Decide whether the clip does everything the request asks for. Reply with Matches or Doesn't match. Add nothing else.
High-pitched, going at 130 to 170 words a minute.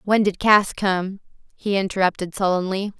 Matches